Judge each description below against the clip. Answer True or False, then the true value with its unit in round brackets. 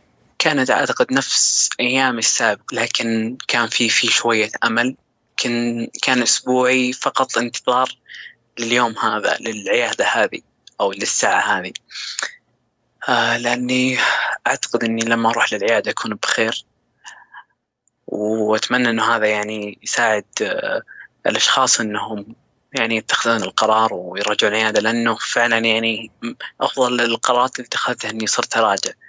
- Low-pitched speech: True (115 Hz)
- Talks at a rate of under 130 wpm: True (115 wpm)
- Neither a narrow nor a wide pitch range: False (1.8 semitones)